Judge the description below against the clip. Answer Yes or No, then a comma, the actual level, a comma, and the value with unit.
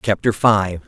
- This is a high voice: No, low, 105 Hz